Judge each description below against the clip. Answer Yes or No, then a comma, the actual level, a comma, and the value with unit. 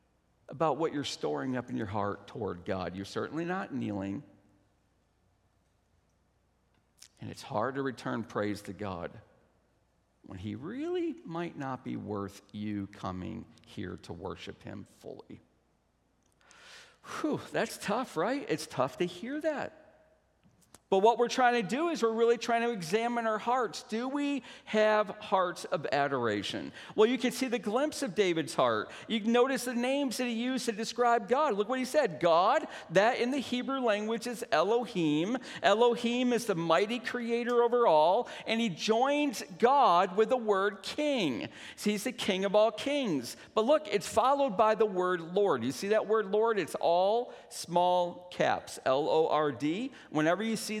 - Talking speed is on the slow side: No, average, 170 wpm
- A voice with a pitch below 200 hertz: No, high, 210 Hz